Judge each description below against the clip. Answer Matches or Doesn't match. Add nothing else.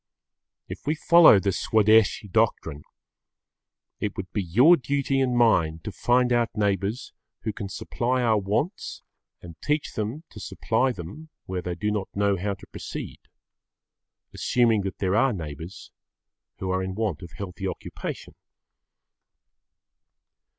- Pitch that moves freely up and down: Doesn't match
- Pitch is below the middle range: Matches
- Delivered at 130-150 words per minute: Matches